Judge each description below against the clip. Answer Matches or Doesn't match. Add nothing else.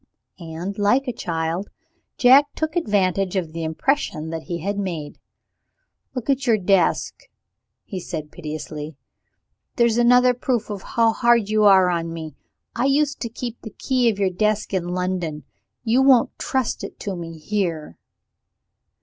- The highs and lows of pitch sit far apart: Matches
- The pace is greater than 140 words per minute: Matches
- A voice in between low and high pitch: Doesn't match